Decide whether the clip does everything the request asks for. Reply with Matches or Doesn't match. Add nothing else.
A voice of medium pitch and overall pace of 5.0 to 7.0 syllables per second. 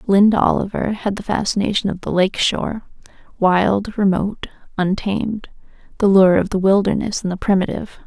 Doesn't match